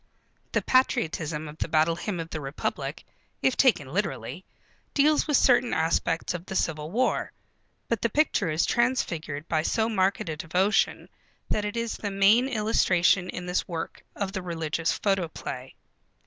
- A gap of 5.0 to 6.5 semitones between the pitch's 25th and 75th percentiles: Yes, average, 5.3 semitones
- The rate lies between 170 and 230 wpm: No, average, 160 wpm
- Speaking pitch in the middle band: Yes, medium, 180 Hz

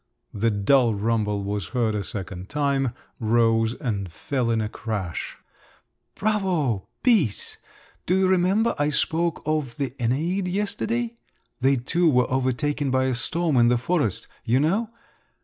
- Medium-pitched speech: No, low, 130 Hz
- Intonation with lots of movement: Yes, wide, 6.9 semitones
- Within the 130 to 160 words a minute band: Yes, average, 145 wpm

